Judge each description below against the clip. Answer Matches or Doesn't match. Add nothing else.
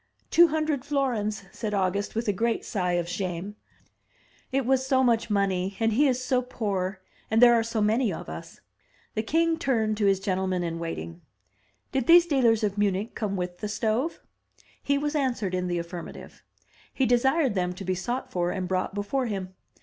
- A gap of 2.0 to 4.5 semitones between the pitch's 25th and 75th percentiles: Doesn't match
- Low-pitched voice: Doesn't match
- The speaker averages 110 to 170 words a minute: Doesn't match